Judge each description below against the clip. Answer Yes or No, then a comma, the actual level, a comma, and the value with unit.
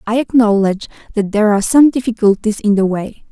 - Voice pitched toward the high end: Yes, high, 220 Hz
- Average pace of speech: Yes, average, 180 wpm